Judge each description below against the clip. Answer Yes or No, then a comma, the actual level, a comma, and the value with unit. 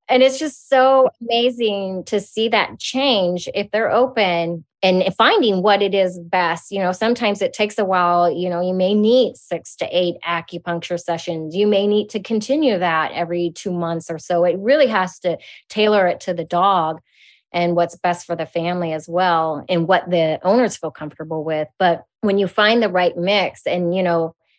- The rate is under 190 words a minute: No, average, 195 wpm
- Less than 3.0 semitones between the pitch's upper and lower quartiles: No, average, 3.6 semitones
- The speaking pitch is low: No, medium, 185 Hz